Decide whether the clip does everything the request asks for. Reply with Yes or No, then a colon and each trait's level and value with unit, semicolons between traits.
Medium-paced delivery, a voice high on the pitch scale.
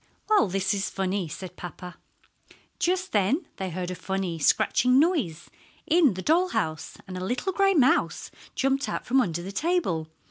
Yes: average, 170 wpm; high, 195 Hz